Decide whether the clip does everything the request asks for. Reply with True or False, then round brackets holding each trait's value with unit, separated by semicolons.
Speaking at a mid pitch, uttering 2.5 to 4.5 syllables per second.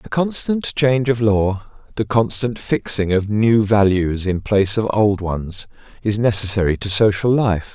False (105 Hz; 4.4 syllables/s)